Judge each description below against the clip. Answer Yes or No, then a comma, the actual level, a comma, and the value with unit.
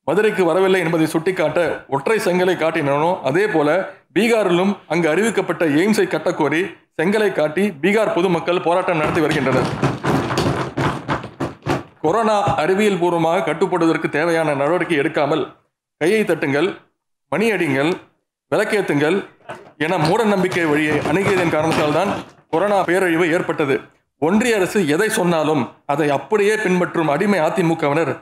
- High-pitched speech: No, medium, 175 Hz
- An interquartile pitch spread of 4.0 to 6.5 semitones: No, average, 3.6 semitones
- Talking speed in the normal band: Yes, average, 110 wpm